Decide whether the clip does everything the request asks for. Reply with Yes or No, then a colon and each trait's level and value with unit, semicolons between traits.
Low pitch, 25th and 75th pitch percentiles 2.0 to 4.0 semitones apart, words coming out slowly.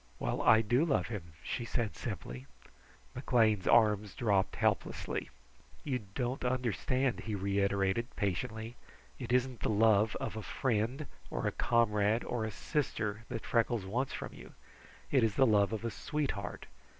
No: low, 110 Hz; average, 3.3 semitones; average, 150 wpm